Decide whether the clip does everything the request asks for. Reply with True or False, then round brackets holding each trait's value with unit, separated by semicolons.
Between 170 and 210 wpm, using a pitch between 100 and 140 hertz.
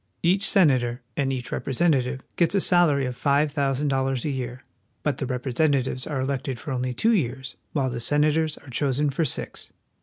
True (180 wpm; 135 Hz)